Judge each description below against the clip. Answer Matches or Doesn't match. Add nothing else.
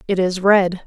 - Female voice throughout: Matches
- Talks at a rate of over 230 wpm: Doesn't match